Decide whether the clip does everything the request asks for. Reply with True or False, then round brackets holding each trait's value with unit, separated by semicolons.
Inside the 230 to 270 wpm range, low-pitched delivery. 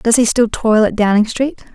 False (240 wpm; 230 Hz)